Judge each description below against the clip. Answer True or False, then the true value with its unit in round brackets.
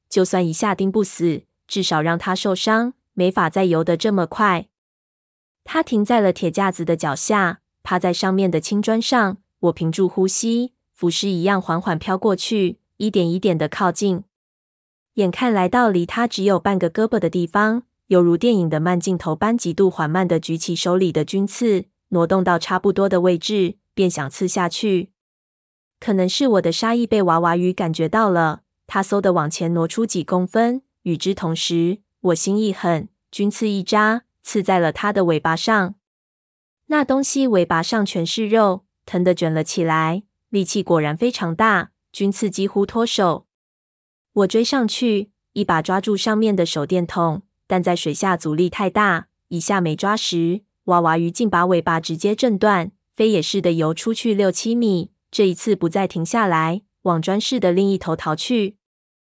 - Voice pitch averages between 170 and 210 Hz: True (190 Hz)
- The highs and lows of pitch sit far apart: False (3.5 semitones)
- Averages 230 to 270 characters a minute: True (250 characters per minute)